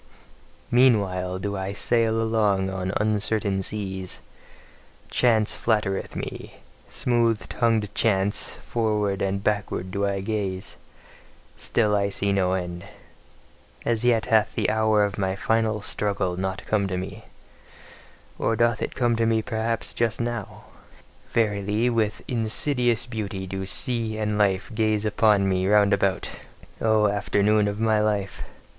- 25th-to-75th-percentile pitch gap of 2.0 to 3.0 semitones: Yes, narrow, 2.4 semitones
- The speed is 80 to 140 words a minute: Yes, slow, 135 wpm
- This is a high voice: No, low, 105 Hz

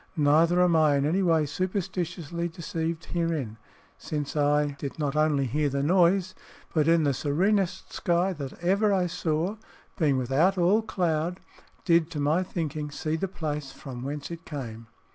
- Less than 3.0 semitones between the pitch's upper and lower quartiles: No, average, 3.3 semitones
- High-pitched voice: No, medium, 160 Hz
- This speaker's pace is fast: No, average, 160 wpm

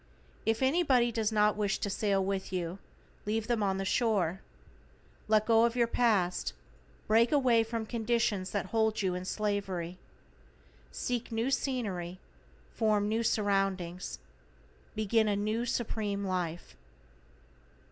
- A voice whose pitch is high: Yes, high, 215 Hz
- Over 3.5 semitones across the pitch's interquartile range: No, average, 3.0 semitones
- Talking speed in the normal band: No, slow, 130 wpm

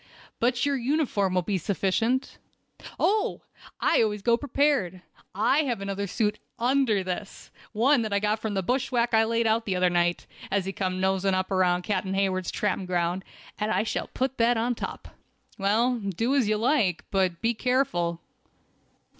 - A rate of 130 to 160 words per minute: No, average, 170 wpm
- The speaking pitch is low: No, high, 210 Hz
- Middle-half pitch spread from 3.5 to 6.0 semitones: Yes, average, 4.3 semitones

